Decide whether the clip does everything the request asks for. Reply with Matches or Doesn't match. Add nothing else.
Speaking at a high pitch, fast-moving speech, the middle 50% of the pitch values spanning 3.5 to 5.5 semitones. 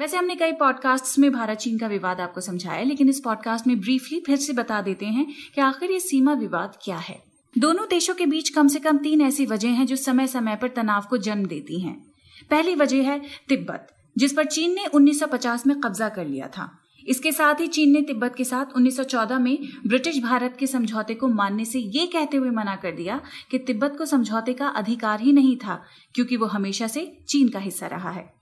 Matches